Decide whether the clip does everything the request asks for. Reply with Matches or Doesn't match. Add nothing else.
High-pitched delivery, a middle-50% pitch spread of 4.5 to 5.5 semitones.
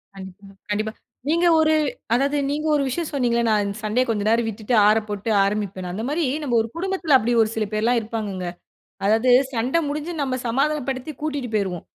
Matches